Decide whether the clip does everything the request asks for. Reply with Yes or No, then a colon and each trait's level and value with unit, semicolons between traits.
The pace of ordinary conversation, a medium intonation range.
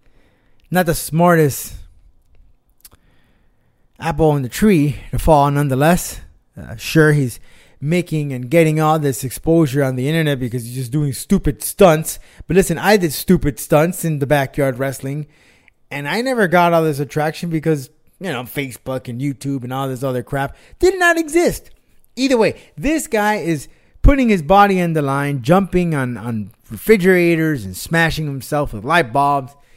Yes: average, 160 wpm; average, 4.5 semitones